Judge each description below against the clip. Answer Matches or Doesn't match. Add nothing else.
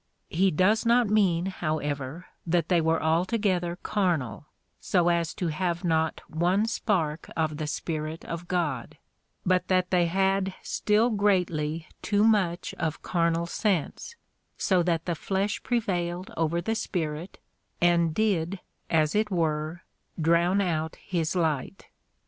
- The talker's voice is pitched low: Doesn't match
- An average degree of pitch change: Matches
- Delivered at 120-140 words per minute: Matches